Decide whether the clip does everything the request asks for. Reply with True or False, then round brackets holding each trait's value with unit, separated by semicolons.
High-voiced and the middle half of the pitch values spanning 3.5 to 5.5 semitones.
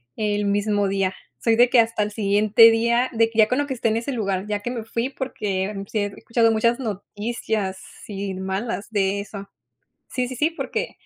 False (220 Hz; 2.6 semitones)